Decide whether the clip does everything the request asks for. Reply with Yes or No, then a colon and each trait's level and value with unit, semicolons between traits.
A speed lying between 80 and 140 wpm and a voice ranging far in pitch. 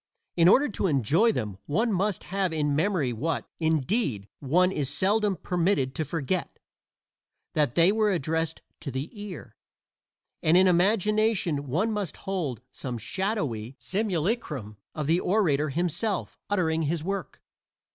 Yes: slow, 135 wpm; wide, 5.7 semitones